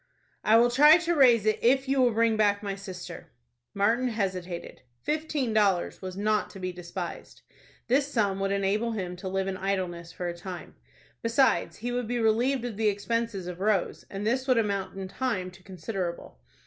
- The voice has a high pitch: Yes, high, 205 Hz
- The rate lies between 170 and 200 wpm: Yes, average, 185 wpm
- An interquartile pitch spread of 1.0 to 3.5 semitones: No, average, 4.2 semitones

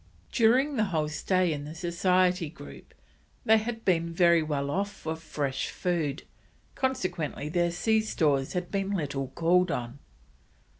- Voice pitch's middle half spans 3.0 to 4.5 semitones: Yes, average, 4.2 semitones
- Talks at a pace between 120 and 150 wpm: Yes, average, 145 wpm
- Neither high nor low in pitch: Yes, medium, 170 Hz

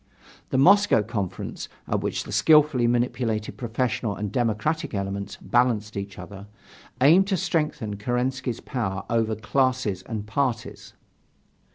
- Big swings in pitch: No, average, 4.0 semitones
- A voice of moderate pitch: No, low, 120 Hz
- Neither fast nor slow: No, slow, 125 wpm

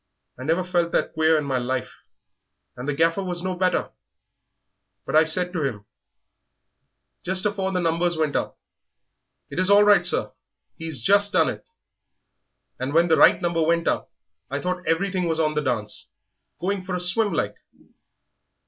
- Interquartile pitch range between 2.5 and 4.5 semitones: Yes, average, 2.9 semitones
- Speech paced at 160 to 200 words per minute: Yes, average, 165 wpm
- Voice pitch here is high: No, medium, 170 Hz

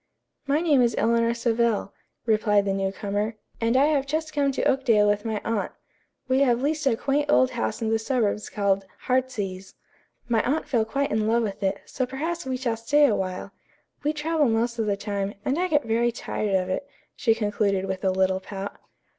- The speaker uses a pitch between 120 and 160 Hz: No, high, 230 Hz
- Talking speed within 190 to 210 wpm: Yes, average, 200 wpm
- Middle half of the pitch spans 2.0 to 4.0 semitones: No, average, 4.7 semitones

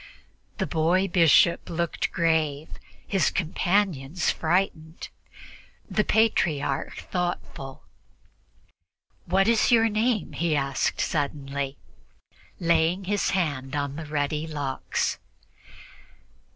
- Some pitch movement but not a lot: Yes, average, 4.5 semitones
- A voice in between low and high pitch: Yes, medium, 165 Hz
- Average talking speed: No, slow, 90 wpm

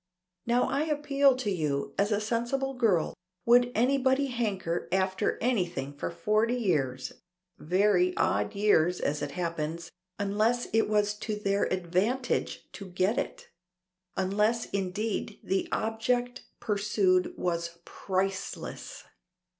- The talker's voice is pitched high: Yes, high, 205 Hz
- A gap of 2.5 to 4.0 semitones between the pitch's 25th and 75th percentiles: No, average, 4.8 semitones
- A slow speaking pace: Yes, slow, 120 wpm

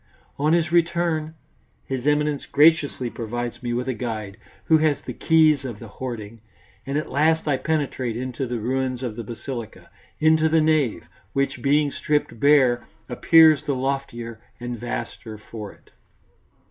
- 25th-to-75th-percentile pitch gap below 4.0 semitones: No, average, 4.3 semitones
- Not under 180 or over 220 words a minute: No, average, 155 wpm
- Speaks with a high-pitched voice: No, low, 135 Hz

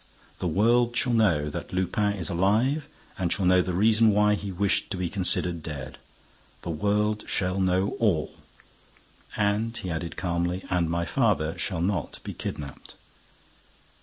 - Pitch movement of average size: Yes, average, 3.4 semitones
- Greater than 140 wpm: Yes, average, 155 wpm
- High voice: No, very low, 95 Hz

